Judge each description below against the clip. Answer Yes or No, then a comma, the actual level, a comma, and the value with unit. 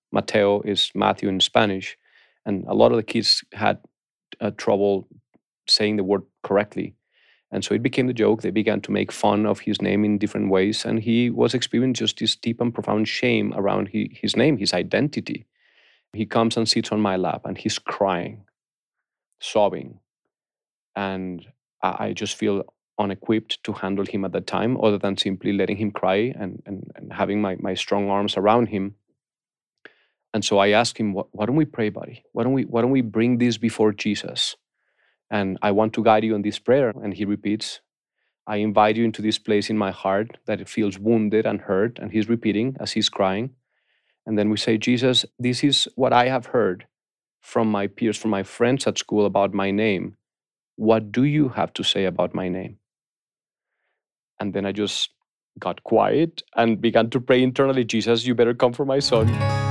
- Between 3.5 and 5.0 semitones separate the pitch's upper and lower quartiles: No, narrow, 2.4 semitones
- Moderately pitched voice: No, low, 105 Hz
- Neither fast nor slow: Yes, average, 195 wpm